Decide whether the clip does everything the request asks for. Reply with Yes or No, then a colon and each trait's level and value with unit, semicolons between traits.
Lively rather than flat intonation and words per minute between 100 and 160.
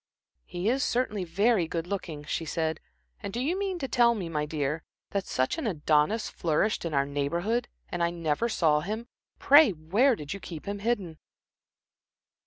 No: wide, 6.8 semitones; average, 180 wpm